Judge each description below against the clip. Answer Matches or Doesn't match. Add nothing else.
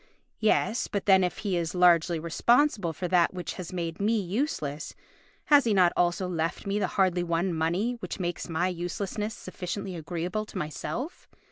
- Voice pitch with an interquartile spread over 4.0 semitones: Doesn't match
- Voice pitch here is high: Doesn't match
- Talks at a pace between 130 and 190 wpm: Matches